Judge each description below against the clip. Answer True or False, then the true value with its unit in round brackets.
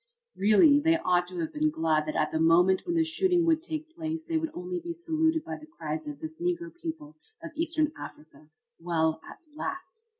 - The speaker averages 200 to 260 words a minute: True (205 wpm)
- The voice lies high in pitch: True (320 Hz)